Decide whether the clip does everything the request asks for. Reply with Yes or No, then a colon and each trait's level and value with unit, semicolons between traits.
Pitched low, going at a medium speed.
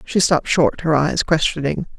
No: medium, 155 Hz; average, 180 wpm